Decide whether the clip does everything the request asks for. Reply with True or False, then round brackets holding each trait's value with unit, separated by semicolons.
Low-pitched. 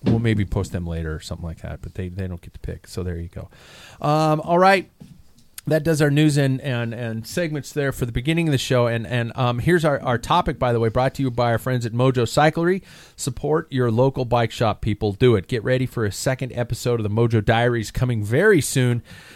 True (125 Hz)